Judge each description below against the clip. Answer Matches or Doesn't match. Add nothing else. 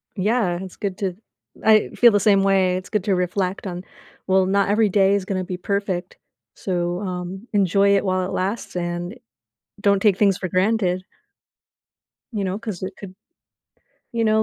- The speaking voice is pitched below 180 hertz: Doesn't match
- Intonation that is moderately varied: Doesn't match